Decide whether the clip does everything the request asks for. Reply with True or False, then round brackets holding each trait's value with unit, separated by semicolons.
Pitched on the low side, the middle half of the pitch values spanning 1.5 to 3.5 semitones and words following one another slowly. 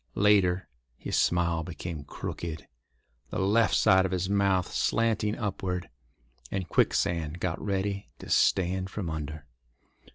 True (95 Hz; 2.6 semitones; 125 wpm)